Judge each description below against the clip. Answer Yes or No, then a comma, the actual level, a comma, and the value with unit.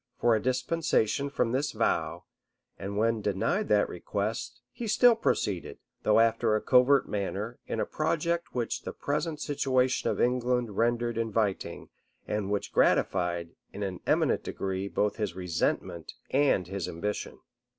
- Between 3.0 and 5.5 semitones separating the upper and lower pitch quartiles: Yes, average, 4.4 semitones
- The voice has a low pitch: Yes, low, 115 Hz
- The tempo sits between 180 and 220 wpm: No, average, 145 wpm